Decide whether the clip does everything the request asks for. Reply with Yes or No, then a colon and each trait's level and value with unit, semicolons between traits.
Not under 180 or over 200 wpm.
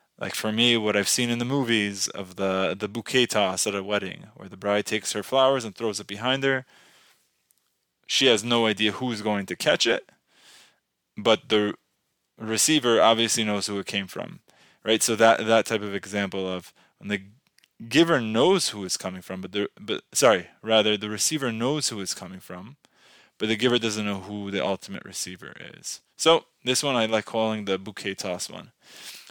Yes: average, 190 wpm